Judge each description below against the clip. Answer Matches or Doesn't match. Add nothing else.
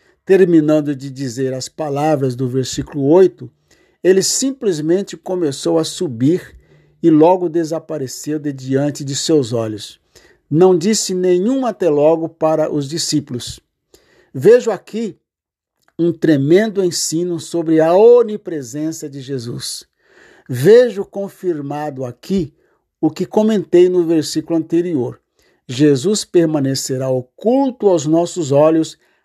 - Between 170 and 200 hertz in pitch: Doesn't match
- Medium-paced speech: Doesn't match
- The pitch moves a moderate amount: Matches